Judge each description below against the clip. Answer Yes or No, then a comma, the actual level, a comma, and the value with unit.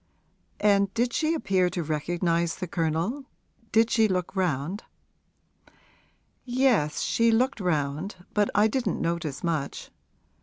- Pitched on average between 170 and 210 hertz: Yes, medium, 185 Hz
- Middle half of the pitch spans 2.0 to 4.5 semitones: No, average, 5.2 semitones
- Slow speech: Yes, slow, 120 wpm